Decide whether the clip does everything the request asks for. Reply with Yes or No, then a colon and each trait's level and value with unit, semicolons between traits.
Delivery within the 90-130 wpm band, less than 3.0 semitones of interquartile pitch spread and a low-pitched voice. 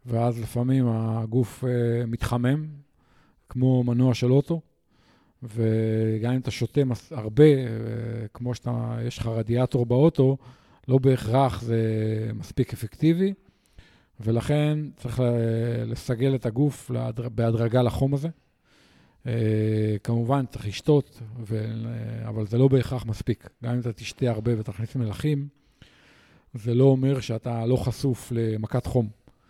Yes: average, 115 wpm; narrow, 2.5 semitones; low, 120 Hz